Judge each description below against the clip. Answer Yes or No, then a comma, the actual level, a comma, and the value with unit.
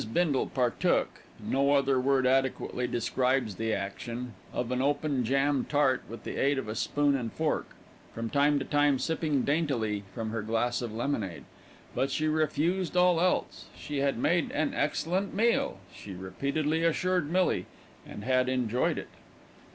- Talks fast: No, average, 160 wpm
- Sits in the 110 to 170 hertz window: Yes, low, 135 Hz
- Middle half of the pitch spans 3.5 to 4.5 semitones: Yes, average, 4.0 semitones